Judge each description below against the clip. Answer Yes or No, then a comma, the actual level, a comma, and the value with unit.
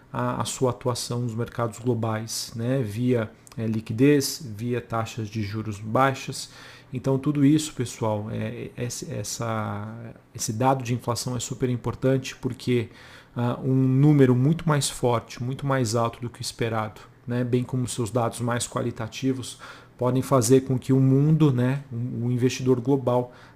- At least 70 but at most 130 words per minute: No, average, 160 wpm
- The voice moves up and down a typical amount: No, narrow, 2.2 semitones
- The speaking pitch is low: Yes, low, 125 Hz